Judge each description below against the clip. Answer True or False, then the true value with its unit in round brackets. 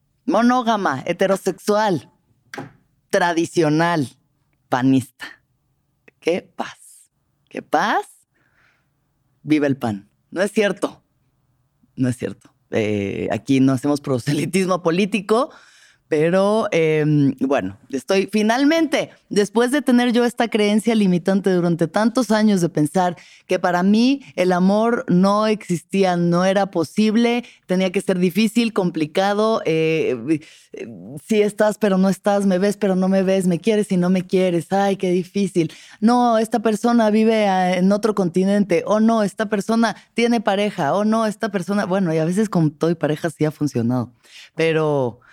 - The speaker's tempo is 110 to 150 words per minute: True (145 wpm)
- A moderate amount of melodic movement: False (5.7 semitones)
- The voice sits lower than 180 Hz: False (190 Hz)